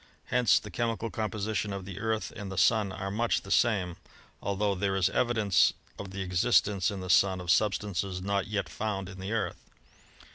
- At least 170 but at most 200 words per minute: Yes, average, 185 wpm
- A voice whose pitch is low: Yes, low, 100 Hz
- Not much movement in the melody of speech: Yes, narrow, 2.3 semitones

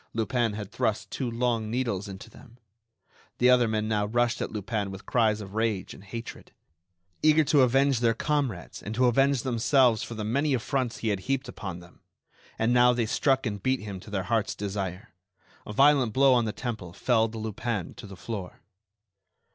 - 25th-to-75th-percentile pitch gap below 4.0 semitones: Yes, average, 3.3 semitones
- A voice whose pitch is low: Yes, low, 115 Hz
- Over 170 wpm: Yes, average, 185 wpm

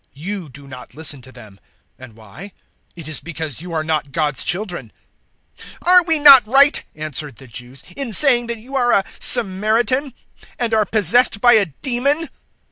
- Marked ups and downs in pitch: Yes, wide, 8.9 semitones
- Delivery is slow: No, average, 175 wpm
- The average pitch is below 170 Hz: No, high, 195 Hz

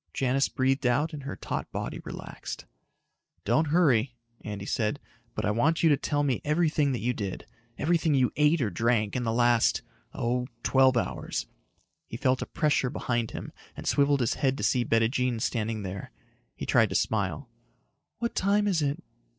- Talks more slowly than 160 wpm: No, average, 175 wpm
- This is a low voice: Yes, low, 130 Hz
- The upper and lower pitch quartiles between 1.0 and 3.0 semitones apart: No, average, 4.0 semitones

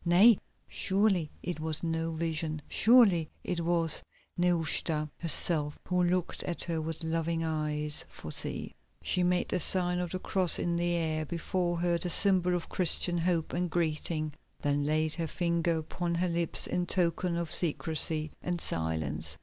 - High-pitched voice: No, medium, 170 Hz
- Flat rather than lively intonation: Yes, narrow, 2.0 semitones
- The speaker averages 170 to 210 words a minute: No, average, 160 wpm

